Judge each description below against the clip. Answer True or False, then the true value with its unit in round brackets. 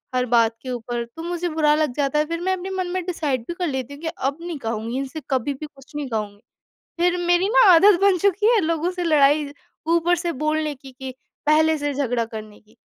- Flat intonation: False (5.0 semitones)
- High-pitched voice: True (300 Hz)